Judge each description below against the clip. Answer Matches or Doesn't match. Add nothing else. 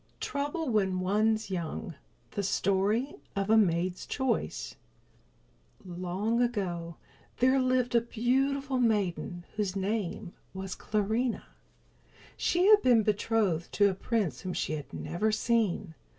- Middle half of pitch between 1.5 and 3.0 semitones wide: Doesn't match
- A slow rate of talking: Matches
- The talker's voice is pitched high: Matches